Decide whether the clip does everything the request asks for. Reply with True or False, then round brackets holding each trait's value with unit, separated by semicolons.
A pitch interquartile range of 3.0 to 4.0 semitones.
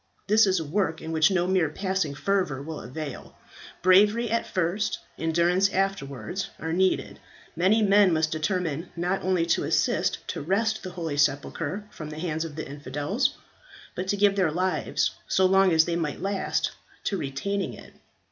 True (3.7 semitones)